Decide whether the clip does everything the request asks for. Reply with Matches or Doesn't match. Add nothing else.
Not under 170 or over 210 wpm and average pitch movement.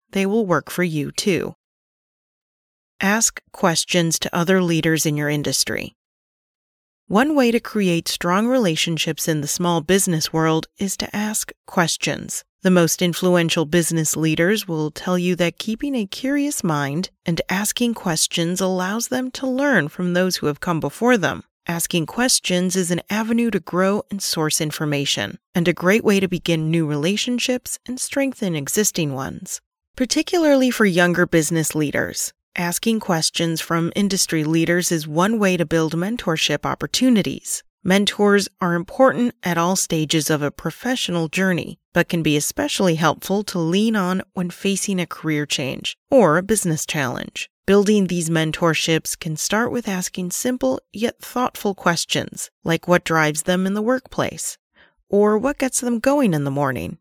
Doesn't match